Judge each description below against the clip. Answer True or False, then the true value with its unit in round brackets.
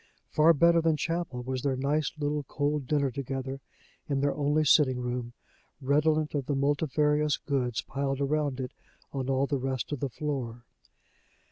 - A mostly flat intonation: True (2.3 semitones)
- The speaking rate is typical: True (160 wpm)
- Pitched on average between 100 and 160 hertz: True (140 Hz)